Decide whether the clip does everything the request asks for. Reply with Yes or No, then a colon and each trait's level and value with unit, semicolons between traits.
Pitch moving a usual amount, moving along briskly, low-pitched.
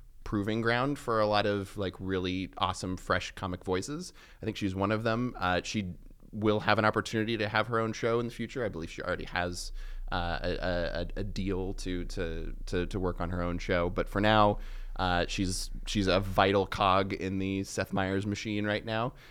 Yes: average, 3.0 semitones; fast, 210 wpm; low, 100 Hz